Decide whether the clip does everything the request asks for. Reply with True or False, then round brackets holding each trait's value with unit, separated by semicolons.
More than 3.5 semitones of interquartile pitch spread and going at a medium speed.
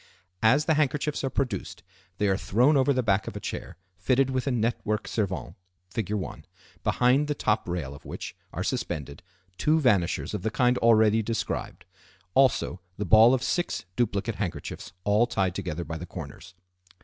True (5.1 semitones; 175 wpm)